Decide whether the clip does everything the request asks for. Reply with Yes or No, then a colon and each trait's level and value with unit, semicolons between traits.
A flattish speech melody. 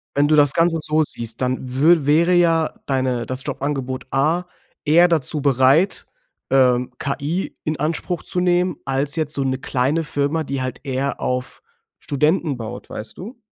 No: average, 3.8 semitones